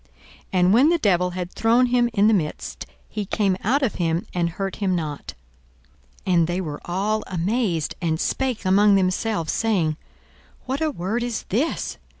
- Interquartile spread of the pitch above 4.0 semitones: Yes, average, 4.5 semitones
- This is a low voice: No, high, 195 Hz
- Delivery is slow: No, average, 170 wpm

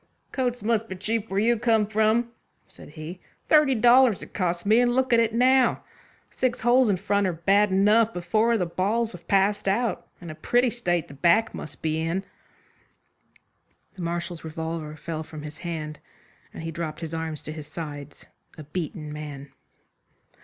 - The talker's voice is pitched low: No, high, 190 Hz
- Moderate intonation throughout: No, wide, 6.0 semitones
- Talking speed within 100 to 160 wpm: No, average, 185 wpm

